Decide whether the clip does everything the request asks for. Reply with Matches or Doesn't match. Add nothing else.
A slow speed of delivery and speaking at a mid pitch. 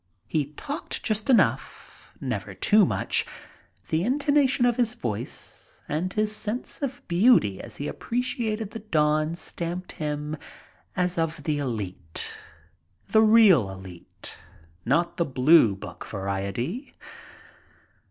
Matches